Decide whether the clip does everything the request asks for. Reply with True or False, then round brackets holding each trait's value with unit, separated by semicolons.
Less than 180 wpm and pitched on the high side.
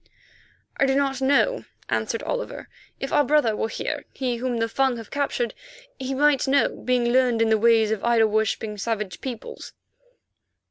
True (170 wpm; 245 Hz)